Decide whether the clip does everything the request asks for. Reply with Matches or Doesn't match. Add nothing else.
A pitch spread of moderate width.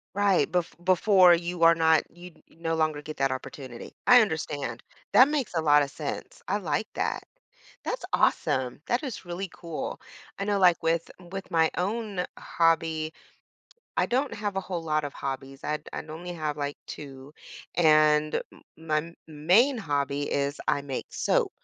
Matches